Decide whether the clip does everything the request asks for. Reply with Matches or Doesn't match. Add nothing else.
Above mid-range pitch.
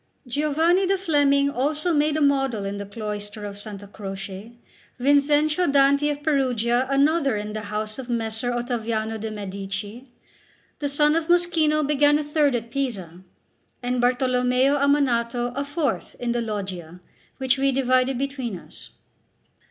Matches